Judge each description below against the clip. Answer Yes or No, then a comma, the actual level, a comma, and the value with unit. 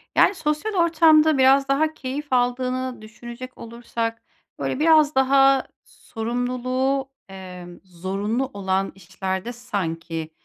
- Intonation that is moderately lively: No, wide, 5.7 semitones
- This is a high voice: Yes, very high, 250 Hz